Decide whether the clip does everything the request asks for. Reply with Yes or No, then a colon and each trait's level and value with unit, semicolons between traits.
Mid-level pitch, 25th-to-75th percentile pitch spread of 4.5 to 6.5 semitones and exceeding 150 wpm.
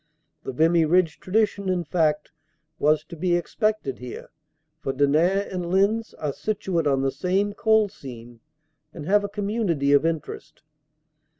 No: medium, 170 Hz; average, 5.2 semitones; average, 145 wpm